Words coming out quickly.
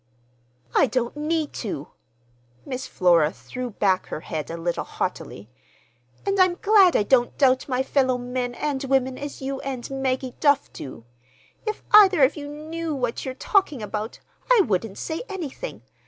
No: average, 160 wpm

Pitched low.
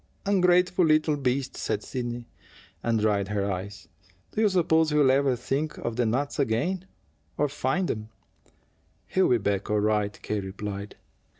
Yes: low, 125 Hz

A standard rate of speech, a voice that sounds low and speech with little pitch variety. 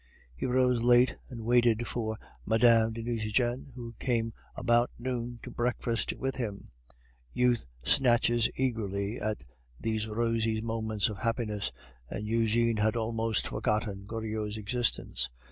No: slow, 130 wpm; low, 115 Hz; narrow, 1.6 semitones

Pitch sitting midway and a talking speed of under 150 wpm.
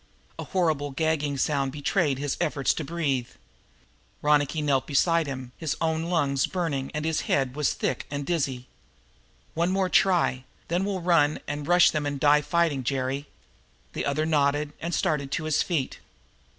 No: medium, 150 Hz; average, 165 wpm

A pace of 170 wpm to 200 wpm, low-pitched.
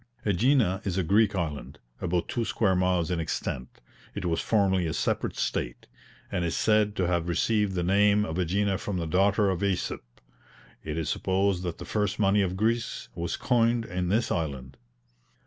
Yes: average, 180 wpm; very low, 95 Hz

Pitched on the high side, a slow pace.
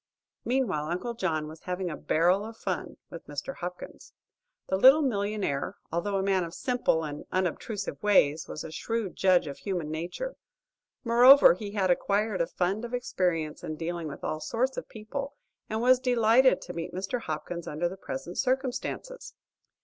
No: high, 195 Hz; average, 170 wpm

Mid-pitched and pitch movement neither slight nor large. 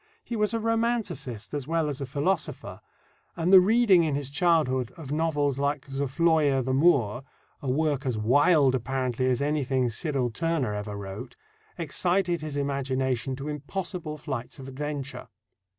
Yes: medium, 145 Hz; average, 4.0 semitones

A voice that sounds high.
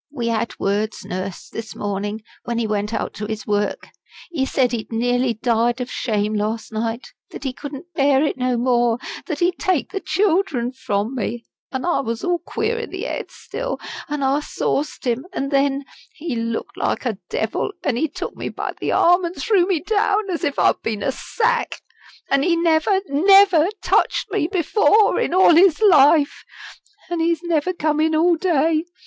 Yes: very high, 280 Hz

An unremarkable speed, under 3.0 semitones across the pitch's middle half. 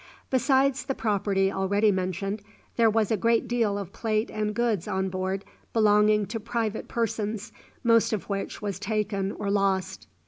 Yes: average, 160 wpm; narrow, 2.4 semitones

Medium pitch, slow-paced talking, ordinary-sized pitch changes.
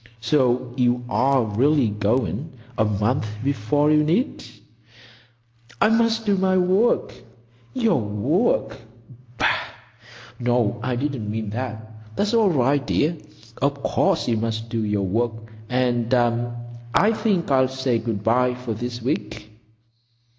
No: low, 125 Hz; slow, 120 wpm; average, 4.2 semitones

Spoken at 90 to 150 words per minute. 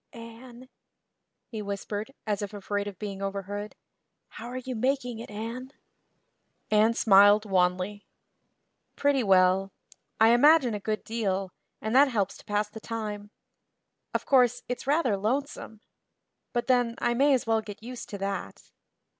Yes: average, 145 wpm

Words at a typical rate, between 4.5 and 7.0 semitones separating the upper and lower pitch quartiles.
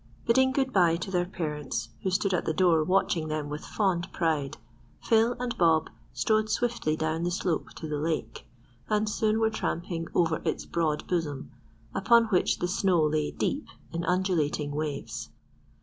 Yes: average, 165 wpm; average, 4.9 semitones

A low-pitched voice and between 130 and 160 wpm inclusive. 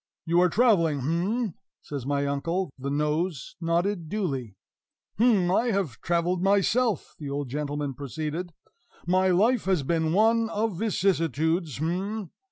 No: medium, 170 Hz; slow, 135 wpm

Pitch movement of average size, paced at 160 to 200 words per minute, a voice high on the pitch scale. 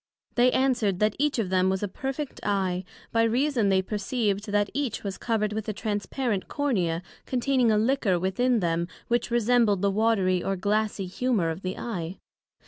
Yes: average, 4.2 semitones; average, 175 wpm; high, 210 Hz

